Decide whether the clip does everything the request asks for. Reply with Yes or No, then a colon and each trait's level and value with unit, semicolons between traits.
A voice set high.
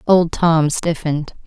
No: medium, 160 Hz